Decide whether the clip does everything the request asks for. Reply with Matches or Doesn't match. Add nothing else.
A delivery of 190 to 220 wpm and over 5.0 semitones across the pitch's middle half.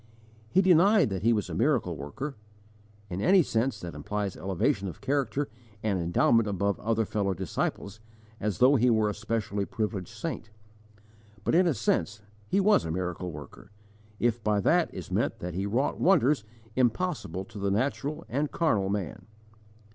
Doesn't match